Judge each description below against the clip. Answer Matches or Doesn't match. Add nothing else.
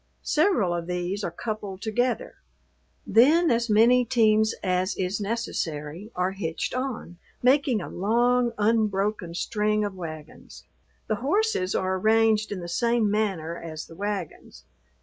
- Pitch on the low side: Doesn't match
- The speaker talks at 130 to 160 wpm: Matches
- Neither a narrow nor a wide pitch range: Matches